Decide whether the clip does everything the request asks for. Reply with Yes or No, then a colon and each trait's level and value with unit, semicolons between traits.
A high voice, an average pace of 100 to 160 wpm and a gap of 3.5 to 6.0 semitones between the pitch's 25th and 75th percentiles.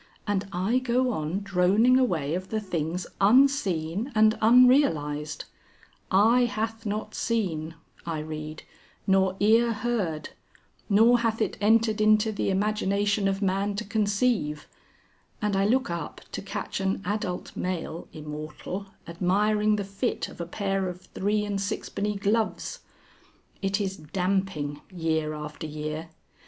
Yes: high, 195 Hz; slow, 135 wpm; average, 4.1 semitones